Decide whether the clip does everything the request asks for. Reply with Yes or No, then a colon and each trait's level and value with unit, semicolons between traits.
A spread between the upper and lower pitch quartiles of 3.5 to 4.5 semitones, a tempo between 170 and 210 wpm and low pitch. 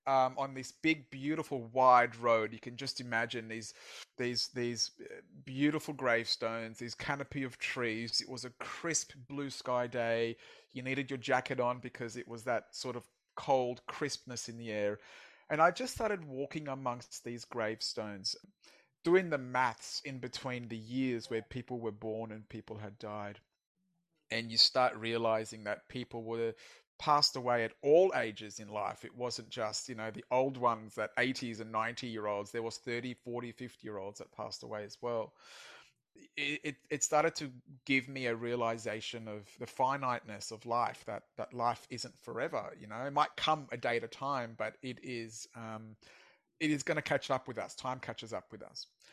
No: average, 2.8 semitones; average, 185 wpm; low, 120 Hz